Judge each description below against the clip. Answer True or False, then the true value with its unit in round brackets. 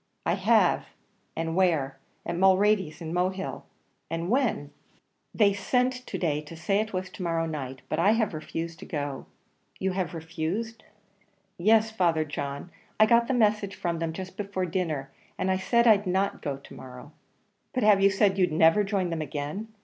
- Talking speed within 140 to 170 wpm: False (180 wpm)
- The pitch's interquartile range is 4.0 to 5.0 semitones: True (4.3 semitones)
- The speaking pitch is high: False (180 Hz)